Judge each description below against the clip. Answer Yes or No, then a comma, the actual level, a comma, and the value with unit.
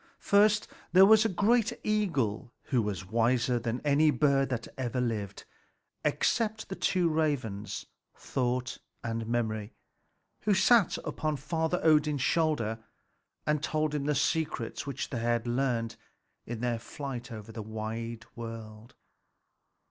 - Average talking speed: No, slow, 130 wpm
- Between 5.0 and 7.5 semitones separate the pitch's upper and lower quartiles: Yes, wide, 5.4 semitones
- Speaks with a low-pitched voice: Yes, low, 125 Hz